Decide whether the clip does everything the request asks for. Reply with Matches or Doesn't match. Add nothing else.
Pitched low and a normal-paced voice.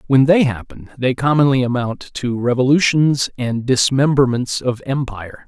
Doesn't match